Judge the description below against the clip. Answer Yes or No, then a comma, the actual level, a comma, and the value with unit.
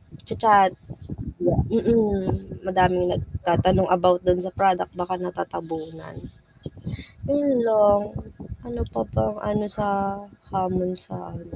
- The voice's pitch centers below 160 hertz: No, medium, 185 Hz